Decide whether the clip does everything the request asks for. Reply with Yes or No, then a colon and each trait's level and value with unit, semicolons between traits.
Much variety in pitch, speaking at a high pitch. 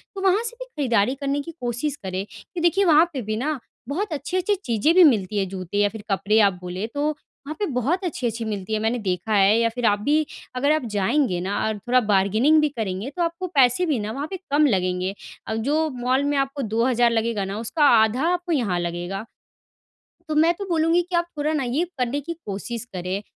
Yes: wide, 6.7 semitones; very high, 250 Hz